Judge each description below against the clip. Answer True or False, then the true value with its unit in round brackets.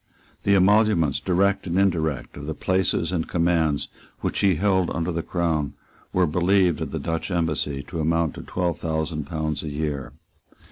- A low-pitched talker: True (85 Hz)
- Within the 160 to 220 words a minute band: True (170 wpm)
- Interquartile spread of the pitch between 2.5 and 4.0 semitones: True (2.9 semitones)